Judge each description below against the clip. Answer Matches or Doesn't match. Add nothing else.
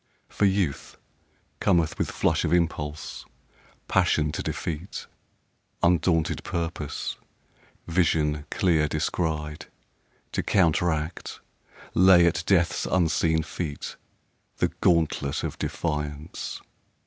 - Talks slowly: Matches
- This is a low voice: Matches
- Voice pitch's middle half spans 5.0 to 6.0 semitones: Doesn't match